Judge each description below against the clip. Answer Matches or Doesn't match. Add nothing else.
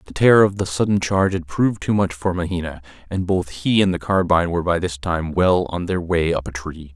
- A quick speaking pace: Matches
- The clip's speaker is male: Matches